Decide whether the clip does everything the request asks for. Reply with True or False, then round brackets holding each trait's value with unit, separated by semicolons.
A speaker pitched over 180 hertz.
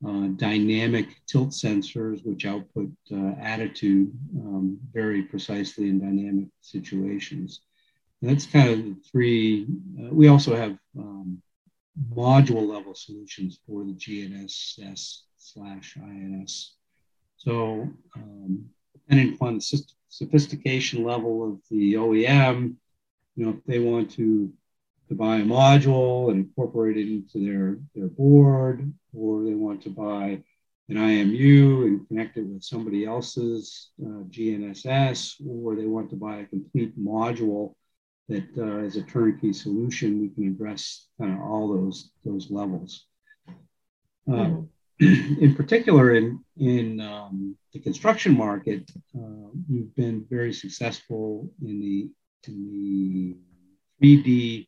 False (110 Hz)